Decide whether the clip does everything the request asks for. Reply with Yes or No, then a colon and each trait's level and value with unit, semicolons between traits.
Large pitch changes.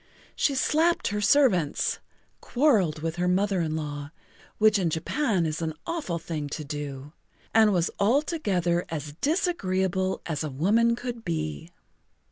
Yes: wide, 6.6 semitones